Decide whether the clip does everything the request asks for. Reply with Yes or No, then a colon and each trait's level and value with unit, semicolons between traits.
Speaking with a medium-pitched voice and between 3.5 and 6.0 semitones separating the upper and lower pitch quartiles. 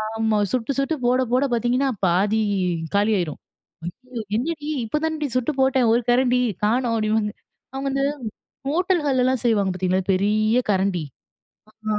No: high, 235 Hz; average, 4.1 semitones